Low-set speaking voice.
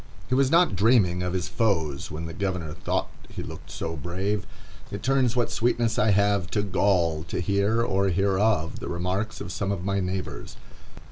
Yes: low, 100 Hz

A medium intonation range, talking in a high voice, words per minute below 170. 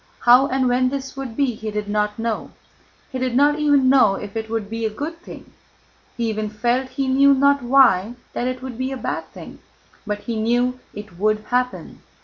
No: average, 3.6 semitones; high, 245 Hz; fast, 205 wpm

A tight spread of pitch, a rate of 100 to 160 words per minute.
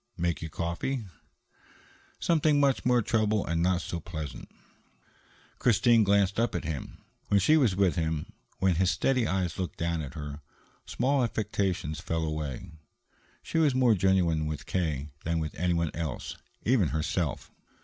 No: average, 5.3 semitones; average, 150 wpm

